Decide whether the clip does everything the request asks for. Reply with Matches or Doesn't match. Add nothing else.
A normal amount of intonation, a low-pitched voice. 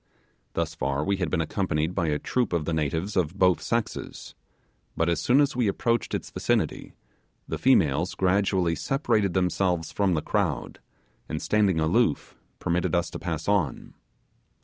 Matches